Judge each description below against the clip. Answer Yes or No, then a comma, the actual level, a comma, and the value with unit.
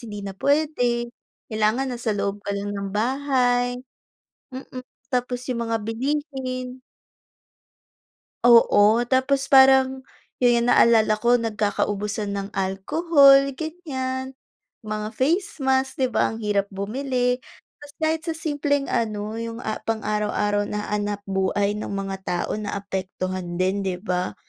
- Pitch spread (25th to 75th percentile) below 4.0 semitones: No, average, 4.3 semitones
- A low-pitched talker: No, high, 235 Hz